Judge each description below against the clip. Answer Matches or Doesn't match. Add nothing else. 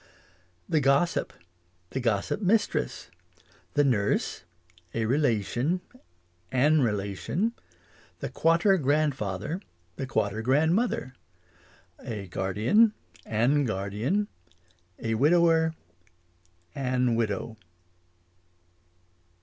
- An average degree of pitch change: Doesn't match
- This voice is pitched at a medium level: Doesn't match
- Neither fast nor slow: Doesn't match